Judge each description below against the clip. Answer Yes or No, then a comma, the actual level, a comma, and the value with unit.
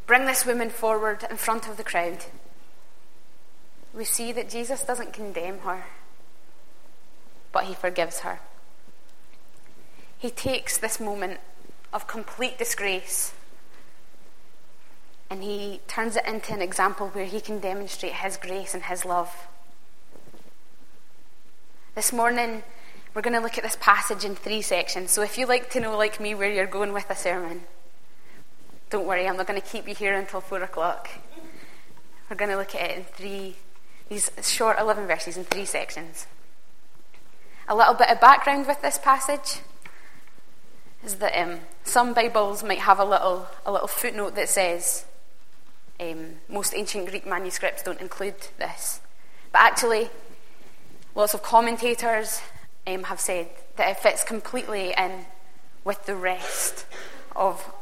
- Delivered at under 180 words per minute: Yes, average, 150 wpm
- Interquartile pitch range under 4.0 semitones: Yes, average, 3.4 semitones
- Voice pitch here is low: No, high, 205 Hz